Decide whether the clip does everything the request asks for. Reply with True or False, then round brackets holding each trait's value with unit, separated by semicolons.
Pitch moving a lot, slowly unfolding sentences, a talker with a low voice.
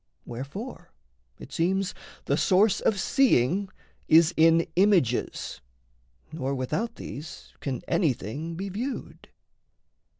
False (6.2 semitones; 100 wpm; 170 Hz)